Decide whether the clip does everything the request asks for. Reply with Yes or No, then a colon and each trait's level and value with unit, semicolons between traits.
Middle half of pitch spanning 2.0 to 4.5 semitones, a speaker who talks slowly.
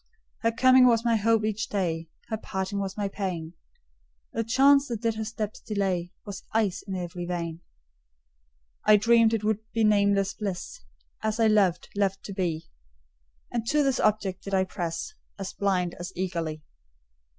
No: average, 3.3 semitones; average, 165 wpm